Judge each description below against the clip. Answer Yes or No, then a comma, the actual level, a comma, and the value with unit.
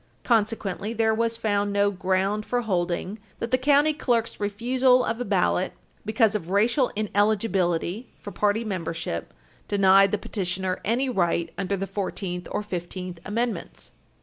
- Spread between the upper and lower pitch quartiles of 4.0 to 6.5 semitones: No, average, 3.3 semitones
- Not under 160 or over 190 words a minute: No, average, 145 wpm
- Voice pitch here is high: Yes, high, 205 Hz